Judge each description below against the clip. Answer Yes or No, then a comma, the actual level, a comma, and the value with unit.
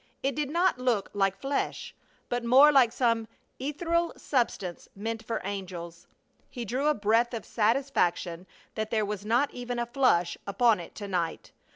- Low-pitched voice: No, high, 230 Hz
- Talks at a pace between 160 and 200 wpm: Yes, average, 165 wpm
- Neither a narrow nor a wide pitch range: Yes, average, 4.9 semitones